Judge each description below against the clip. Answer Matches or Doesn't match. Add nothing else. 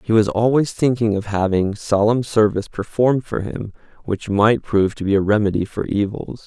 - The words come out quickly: Doesn't match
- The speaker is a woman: Doesn't match